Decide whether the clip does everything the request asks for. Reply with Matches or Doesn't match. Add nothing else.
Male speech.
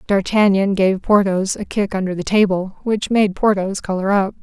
Doesn't match